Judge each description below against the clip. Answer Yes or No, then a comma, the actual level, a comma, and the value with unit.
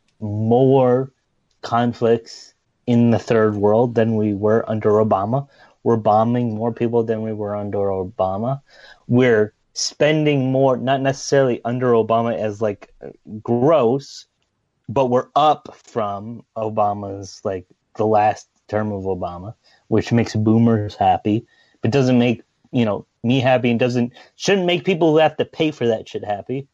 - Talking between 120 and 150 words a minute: Yes, average, 145 wpm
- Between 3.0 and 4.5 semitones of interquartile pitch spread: Yes, average, 3.3 semitones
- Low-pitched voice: Yes, low, 115 Hz